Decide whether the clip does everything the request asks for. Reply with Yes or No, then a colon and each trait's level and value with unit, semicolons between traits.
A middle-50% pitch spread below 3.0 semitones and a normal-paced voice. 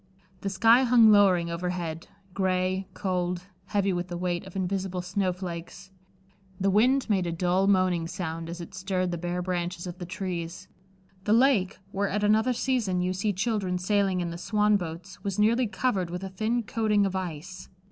Yes: narrow, 2.4 semitones; average, 175 wpm